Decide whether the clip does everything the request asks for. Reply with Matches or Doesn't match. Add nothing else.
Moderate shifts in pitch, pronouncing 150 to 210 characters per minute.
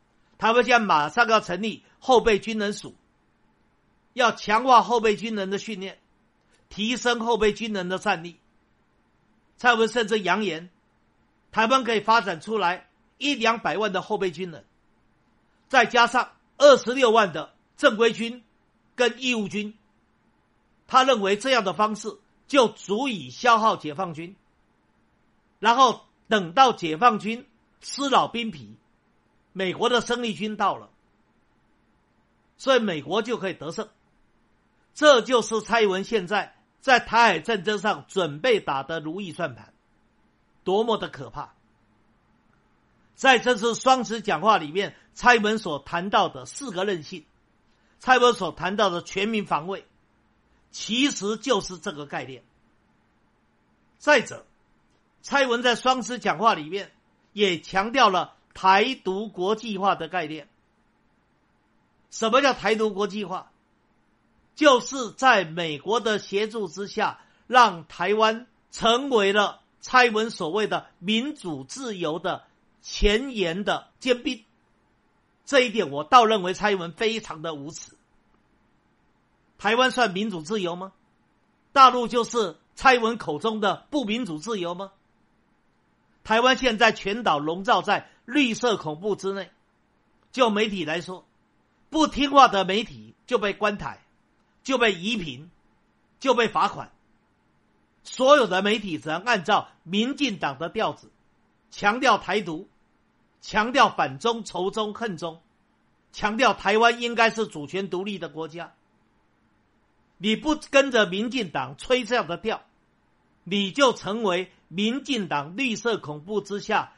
Matches